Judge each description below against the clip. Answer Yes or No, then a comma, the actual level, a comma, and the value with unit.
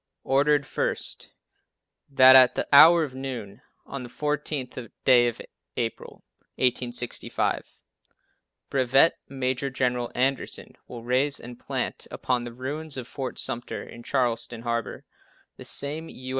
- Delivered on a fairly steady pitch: Yes, narrow, 2.2 semitones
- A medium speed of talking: No, slow, 130 wpm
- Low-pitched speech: Yes, low, 130 Hz